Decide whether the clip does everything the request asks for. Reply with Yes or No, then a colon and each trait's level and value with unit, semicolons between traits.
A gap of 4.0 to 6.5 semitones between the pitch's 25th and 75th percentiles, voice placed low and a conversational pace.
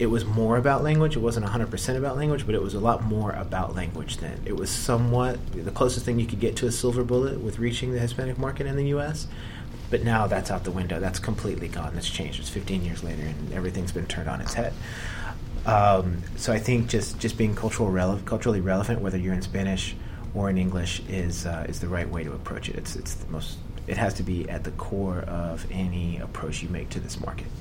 No: average, 4.6 semitones; low, 100 Hz; fast, 235 wpm